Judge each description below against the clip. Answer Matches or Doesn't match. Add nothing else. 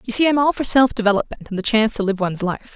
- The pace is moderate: Doesn't match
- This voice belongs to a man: Doesn't match